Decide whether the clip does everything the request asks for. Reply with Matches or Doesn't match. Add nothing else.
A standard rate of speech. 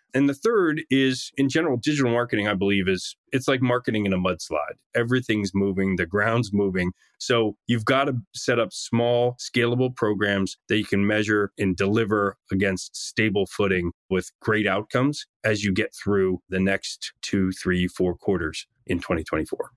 Matches